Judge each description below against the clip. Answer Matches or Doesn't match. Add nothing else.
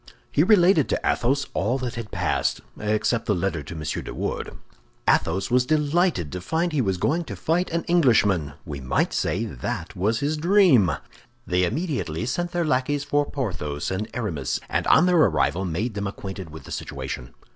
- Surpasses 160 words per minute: Matches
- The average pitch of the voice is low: Matches